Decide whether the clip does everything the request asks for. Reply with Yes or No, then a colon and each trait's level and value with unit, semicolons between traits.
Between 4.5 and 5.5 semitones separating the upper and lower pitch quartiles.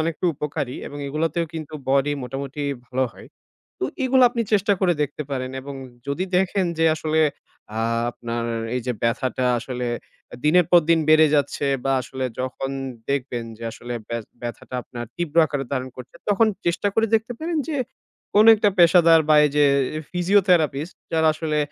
Yes: average, 5.1 semitones